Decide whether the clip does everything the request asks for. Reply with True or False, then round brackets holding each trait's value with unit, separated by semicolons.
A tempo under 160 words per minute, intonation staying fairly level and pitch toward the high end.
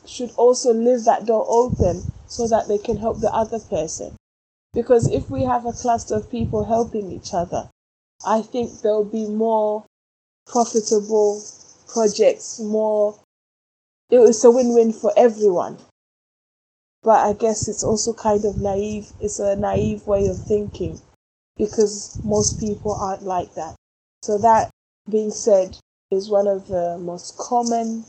True (145 wpm; 1.9 semitones; 215 Hz)